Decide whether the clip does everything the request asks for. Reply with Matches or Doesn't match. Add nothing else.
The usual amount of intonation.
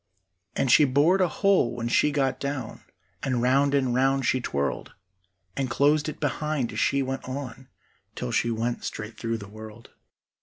Matches